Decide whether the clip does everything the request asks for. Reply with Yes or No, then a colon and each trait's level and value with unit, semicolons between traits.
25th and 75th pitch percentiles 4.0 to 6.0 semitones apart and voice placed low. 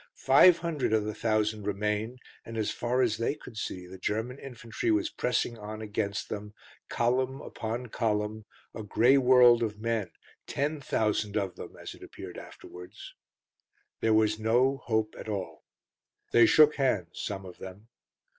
No: average, 3.1 semitones; low, 110 Hz